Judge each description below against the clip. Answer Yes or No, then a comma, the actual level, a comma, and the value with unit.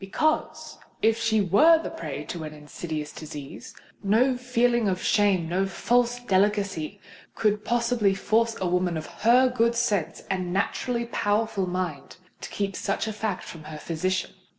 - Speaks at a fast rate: No, average, 150 wpm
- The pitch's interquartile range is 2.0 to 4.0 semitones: No, average, 4.6 semitones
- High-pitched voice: Yes, high, 205 Hz